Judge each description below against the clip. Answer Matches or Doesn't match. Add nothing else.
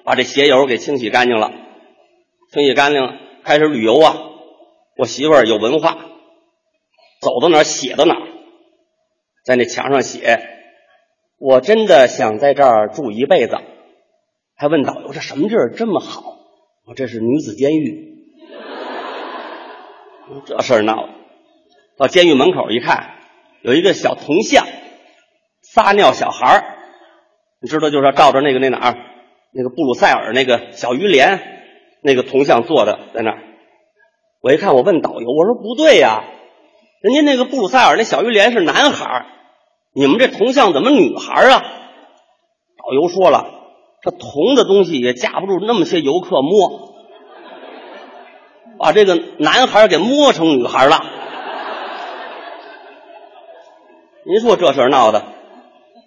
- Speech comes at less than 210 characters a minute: Doesn't match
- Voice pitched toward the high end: Matches